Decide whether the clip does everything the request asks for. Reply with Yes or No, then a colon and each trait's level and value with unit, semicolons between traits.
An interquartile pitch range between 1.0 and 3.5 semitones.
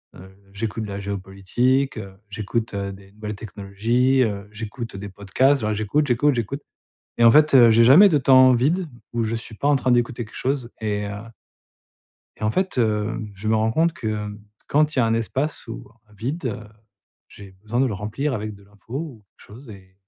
No: average, 4.0 semitones